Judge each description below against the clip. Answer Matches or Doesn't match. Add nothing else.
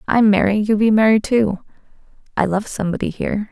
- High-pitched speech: Matches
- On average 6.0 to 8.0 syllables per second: Matches